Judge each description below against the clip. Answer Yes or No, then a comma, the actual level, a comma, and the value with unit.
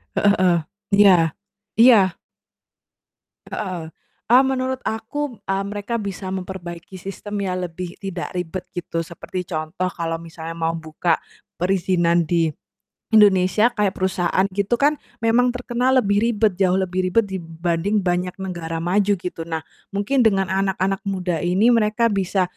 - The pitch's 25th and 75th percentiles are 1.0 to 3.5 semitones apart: Yes, average, 3.1 semitones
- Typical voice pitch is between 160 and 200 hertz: Yes, high, 190 Hz